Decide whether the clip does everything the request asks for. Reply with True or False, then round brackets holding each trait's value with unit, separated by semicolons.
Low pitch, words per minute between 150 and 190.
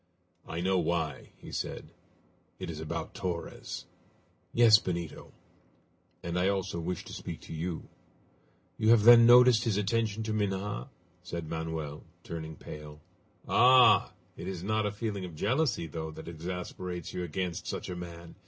True (90 Hz; 155 wpm)